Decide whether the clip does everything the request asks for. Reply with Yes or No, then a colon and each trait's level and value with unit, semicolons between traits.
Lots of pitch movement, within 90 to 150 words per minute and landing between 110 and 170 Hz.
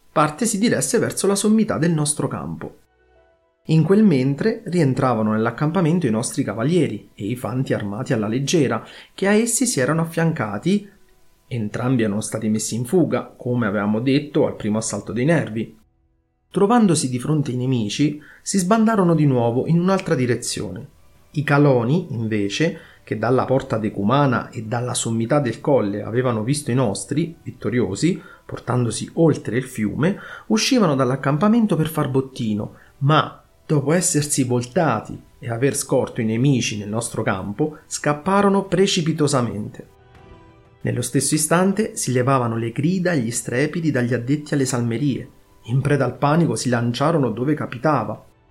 Yes: wide, 5.7 semitones; average, 145 wpm; low, 135 Hz